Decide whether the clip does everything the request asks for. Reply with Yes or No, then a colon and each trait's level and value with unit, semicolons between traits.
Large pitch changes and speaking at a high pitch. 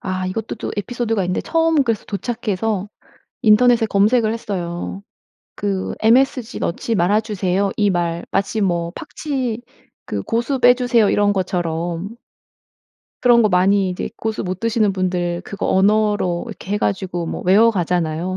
No: average, 3.8 semitones; high, 200 Hz